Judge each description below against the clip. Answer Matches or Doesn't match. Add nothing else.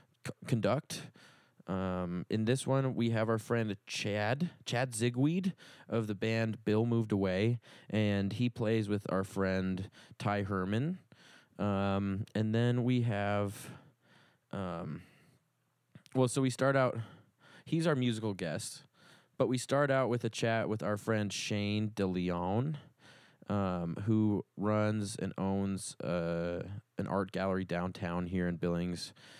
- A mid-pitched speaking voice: Doesn't match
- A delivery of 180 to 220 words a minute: Doesn't match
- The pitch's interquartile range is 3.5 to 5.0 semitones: Matches